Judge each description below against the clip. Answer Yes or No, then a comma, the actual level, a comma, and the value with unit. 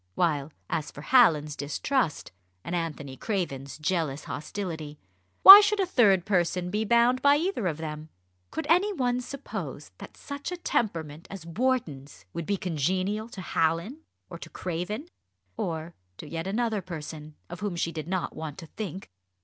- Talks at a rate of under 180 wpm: Yes, average, 160 wpm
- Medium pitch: Yes, medium, 180 Hz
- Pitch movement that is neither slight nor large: No, wide, 7.0 semitones